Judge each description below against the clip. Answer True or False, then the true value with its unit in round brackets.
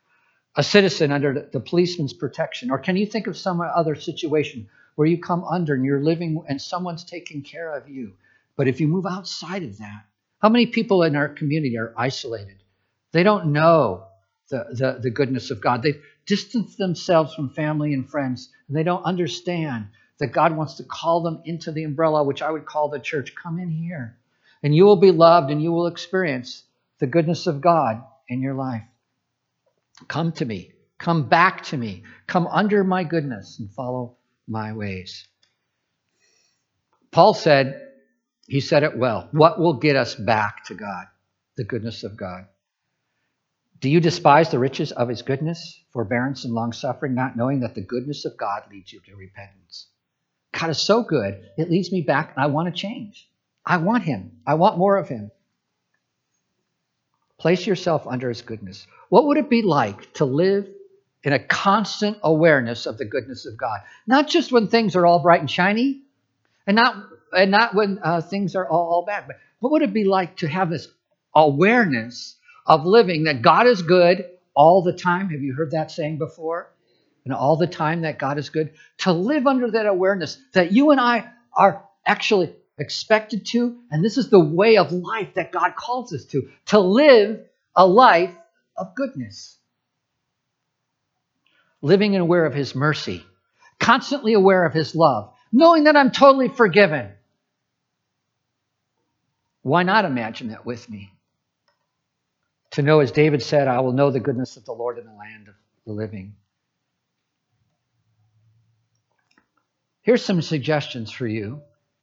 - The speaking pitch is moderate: True (155 Hz)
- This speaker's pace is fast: False (170 wpm)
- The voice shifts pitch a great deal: True (6.6 semitones)